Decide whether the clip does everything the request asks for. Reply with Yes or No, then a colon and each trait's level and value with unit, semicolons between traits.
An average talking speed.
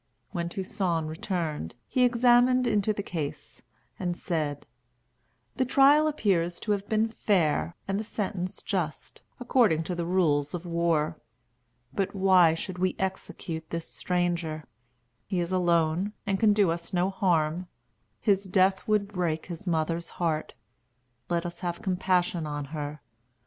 Yes: average, 145 wpm